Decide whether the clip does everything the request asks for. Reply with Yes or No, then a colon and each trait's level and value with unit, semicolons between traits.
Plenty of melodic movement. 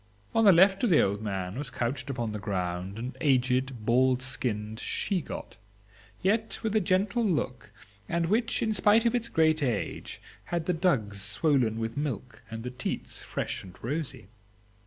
Yes: wide, 8.2 semitones